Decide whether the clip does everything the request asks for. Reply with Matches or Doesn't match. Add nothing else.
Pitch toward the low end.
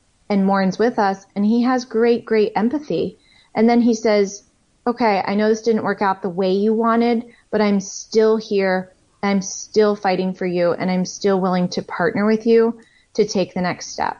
Doesn't match